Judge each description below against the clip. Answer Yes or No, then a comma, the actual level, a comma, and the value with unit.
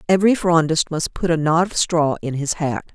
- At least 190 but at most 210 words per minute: No, fast, 225 wpm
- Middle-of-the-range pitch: Yes, medium, 165 Hz